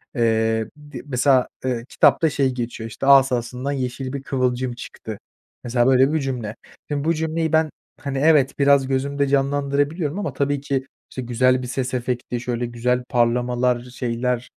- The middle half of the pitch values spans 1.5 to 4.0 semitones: Yes, narrow, 2.5 semitones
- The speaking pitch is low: Yes, low, 130 Hz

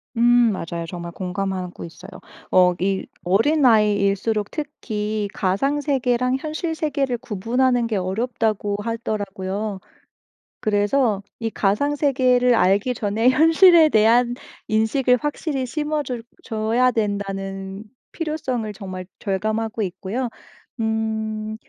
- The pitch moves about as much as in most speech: Yes, average, 4.3 semitones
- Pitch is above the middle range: Yes, high, 220 Hz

